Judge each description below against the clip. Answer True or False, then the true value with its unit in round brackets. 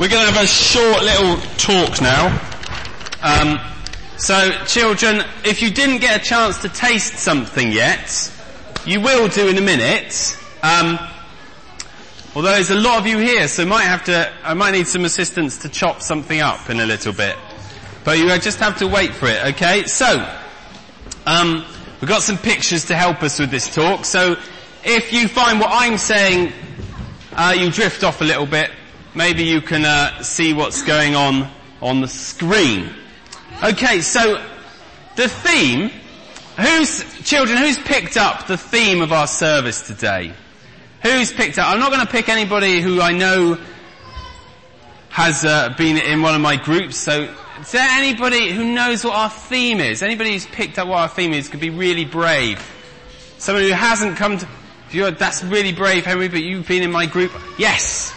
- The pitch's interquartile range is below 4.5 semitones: False (5.2 semitones)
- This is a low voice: False (185 Hz)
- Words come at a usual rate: True (175 wpm)